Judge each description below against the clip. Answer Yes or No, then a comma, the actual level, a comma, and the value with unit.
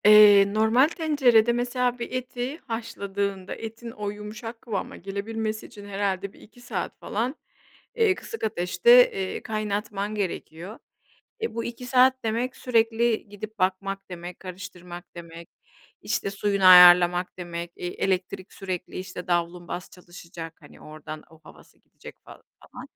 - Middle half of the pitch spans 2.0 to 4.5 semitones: Yes, average, 4.2 semitones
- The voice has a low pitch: No, high, 205 Hz